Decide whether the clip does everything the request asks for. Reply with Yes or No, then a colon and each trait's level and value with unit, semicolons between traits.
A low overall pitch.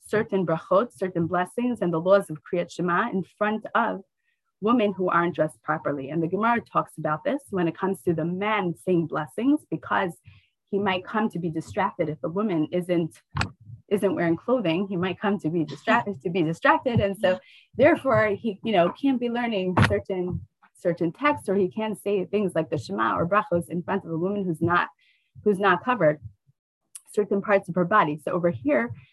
No: medium, 185 Hz